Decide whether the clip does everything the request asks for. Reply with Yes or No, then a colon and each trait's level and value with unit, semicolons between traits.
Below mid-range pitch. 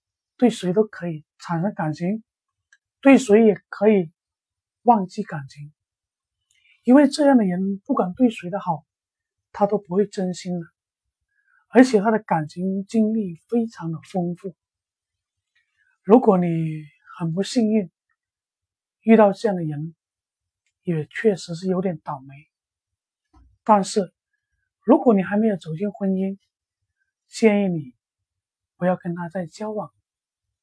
No: high, 190 Hz